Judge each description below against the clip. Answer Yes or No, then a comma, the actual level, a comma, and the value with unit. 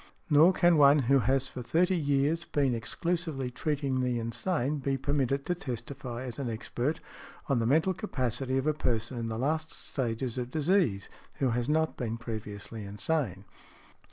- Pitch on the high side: No, low, 135 Hz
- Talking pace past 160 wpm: Yes, average, 170 wpm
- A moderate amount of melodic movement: Yes, average, 4.3 semitones